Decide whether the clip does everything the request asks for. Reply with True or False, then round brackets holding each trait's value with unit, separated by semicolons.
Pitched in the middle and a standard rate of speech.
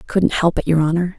False (170 Hz; 305 wpm)